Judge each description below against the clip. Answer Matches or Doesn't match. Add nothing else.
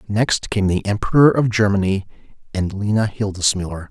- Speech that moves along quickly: Doesn't match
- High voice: Doesn't match